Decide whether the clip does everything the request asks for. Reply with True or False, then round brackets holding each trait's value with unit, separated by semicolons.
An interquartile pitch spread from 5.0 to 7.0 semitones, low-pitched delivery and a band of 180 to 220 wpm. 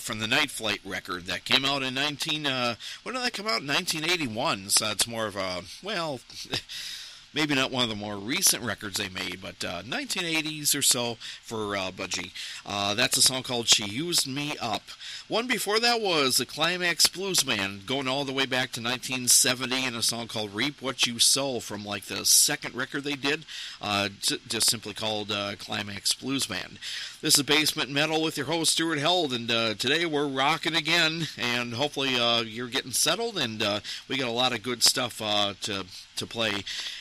True (5.6 semitones; 125 Hz; 200 wpm)